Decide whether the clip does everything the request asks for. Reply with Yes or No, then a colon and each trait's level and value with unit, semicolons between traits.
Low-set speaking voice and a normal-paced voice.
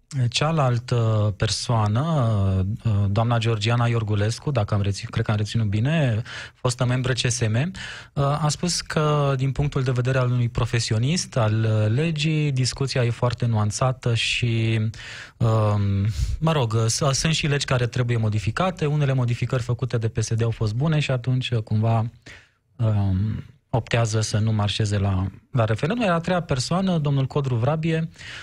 Yes: low, 120 Hz; average, 140 wpm